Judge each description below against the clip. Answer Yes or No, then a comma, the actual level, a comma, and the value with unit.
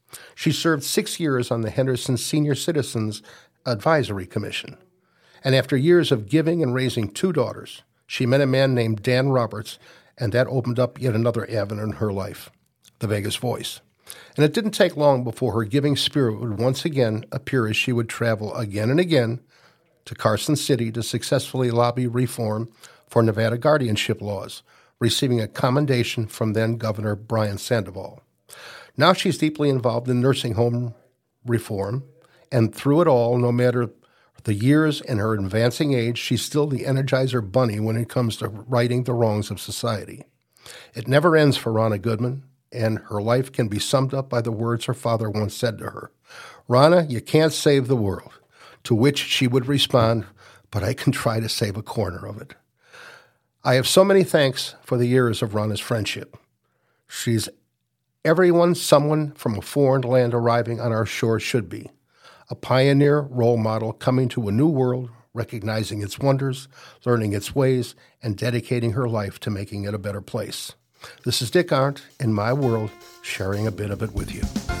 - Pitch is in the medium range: No, low, 120 Hz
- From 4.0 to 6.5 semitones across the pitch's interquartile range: No, average, 3.4 semitones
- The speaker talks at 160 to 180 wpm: Yes, average, 175 wpm